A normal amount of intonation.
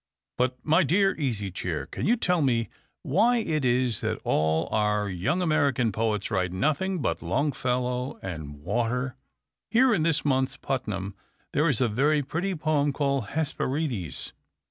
No: wide, 6.7 semitones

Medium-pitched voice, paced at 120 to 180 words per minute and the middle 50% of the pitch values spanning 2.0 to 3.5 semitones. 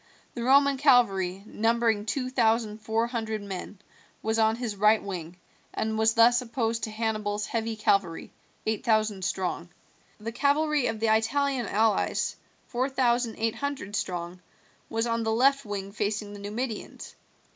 No: high, 220 Hz; average, 150 wpm; narrow, 2.5 semitones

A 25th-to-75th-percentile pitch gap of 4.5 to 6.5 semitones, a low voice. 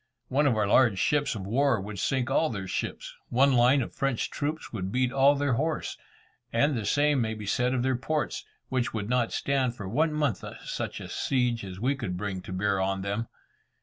Yes: average, 5.0 semitones; low, 125 Hz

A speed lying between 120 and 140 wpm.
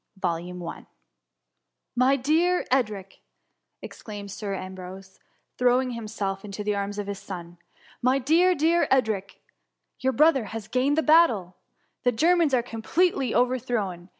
Yes: slow, 135 wpm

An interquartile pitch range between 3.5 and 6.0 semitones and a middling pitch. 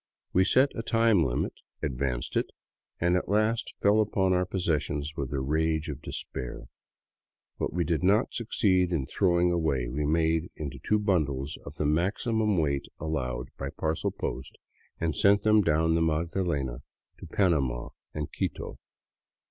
No: average, 4.9 semitones; very low, 80 Hz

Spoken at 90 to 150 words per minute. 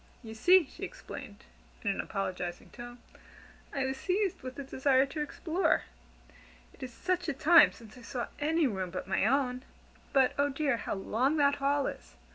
No: average, 180 wpm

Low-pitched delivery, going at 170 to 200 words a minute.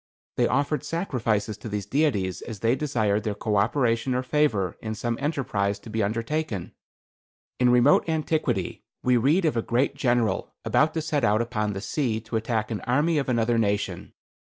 Yes: low, 120 Hz; average, 175 wpm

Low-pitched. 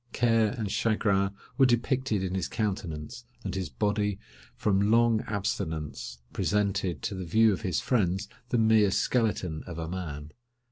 Yes: low, 100 Hz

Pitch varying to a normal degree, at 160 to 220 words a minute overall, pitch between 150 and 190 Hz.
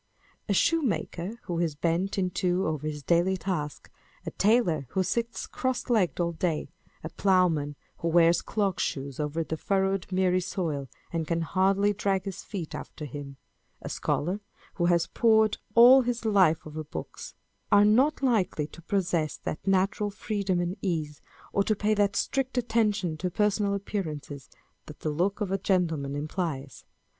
Yes: average, 4.3 semitones; average, 165 wpm; medium, 185 Hz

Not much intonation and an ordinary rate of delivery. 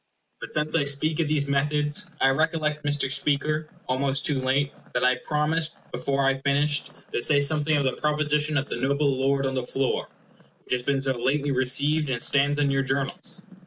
Yes: narrow, 2.0 semitones; average, 195 wpm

